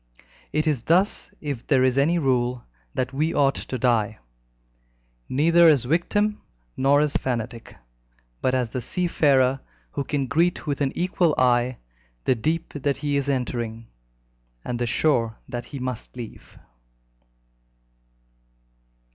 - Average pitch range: Yes, average, 3.7 semitones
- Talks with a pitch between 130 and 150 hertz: Yes, low, 135 Hz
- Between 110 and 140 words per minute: Yes, slow, 135 wpm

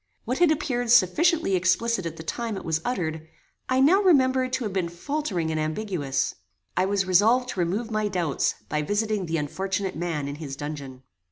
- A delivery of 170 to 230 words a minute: Yes, average, 185 wpm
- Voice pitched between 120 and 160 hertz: No, high, 190 Hz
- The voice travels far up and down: Yes, wide, 7.1 semitones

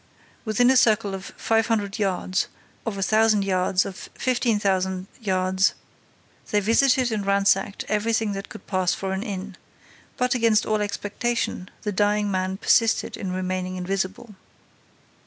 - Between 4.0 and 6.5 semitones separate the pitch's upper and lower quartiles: No, average, 2.8 semitones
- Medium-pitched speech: No, high, 200 Hz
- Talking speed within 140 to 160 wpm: Yes, average, 145 wpm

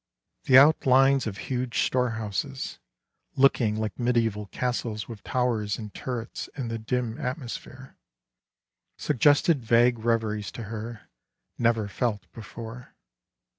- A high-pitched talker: No, low, 120 Hz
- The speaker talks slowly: Yes, slow, 110 wpm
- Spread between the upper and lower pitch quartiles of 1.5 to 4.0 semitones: Yes, narrow, 2.5 semitones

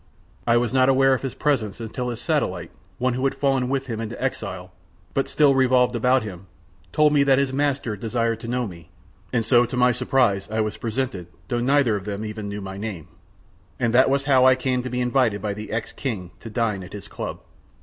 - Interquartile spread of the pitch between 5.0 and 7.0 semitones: No, average, 3.6 semitones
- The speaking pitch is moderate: No, low, 120 Hz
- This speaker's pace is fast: Yes, fast, 220 wpm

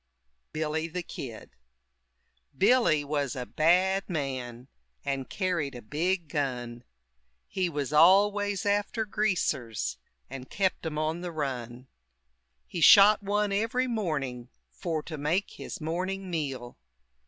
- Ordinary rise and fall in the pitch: No, wide, 6.2 semitones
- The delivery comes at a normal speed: No, slow, 120 wpm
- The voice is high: No, medium, 160 Hz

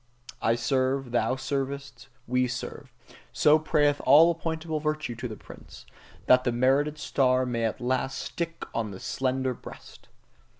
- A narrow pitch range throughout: No, average, 3.2 semitones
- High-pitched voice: No, low, 130 Hz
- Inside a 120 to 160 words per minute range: Yes, average, 145 wpm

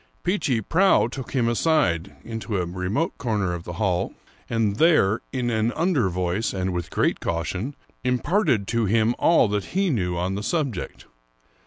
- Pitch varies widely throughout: Yes, wide, 6.1 semitones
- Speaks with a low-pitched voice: Yes, low, 110 Hz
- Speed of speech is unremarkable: Yes, average, 165 wpm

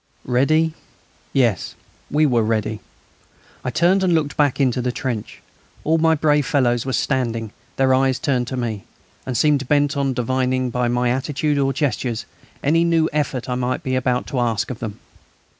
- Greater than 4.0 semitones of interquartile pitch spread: No, average, 3.1 semitones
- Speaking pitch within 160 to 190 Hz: No, low, 130 Hz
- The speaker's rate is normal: Yes, average, 175 wpm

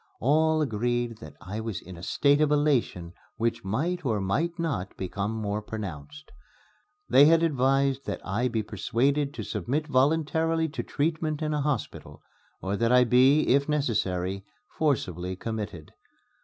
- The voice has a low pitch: Yes, low, 125 Hz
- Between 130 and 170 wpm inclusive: Yes, average, 150 wpm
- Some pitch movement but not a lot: No, wide, 6.5 semitones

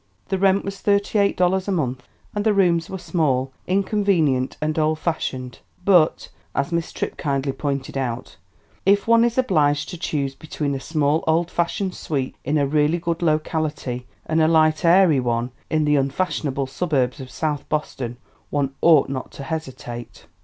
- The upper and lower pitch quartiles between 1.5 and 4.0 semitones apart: No, average, 4.5 semitones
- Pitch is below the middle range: No, medium, 155 Hz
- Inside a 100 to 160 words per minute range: No, average, 170 wpm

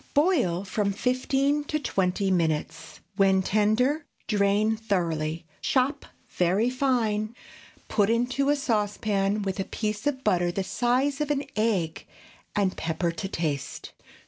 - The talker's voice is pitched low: No, high, 210 Hz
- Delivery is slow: Yes, slow, 130 wpm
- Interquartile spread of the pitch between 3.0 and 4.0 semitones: No, average, 5.2 semitones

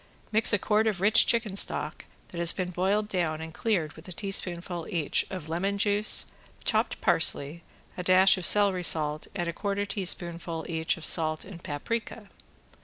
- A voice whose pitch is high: No, medium, 180 Hz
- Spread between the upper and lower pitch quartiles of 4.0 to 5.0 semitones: No, average, 3.4 semitones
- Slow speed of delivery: No, average, 175 wpm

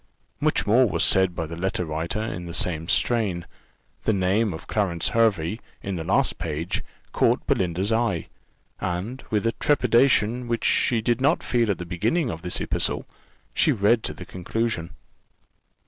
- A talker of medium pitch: No, low, 100 Hz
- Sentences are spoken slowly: No, average, 165 wpm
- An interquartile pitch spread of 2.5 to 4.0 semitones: No, average, 4.9 semitones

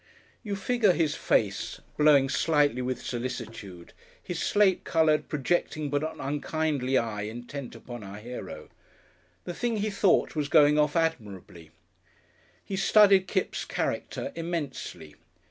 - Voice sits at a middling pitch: Yes, medium, 150 Hz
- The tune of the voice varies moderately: No, wide, 6.0 semitones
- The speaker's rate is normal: No, slow, 130 wpm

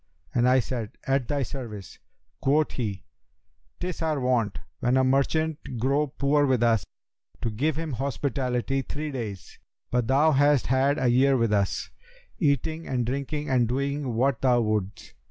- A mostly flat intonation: No, average, 3.0 semitones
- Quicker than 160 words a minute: No, average, 155 wpm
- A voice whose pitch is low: Yes, low, 130 Hz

